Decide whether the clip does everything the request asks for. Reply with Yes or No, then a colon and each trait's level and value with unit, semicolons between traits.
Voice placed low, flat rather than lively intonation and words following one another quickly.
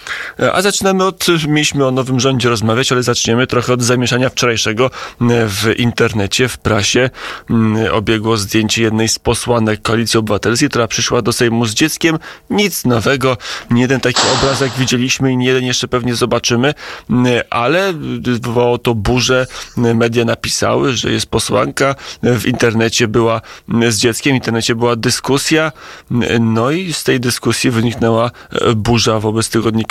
No: low, 120 Hz; narrow, 2.2 semitones; average, 145 wpm